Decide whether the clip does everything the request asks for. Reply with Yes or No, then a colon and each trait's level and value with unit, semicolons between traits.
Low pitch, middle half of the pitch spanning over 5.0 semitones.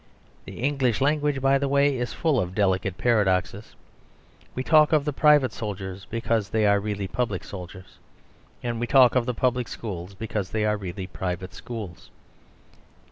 Yes: low, 110 Hz; wide, 5.4 semitones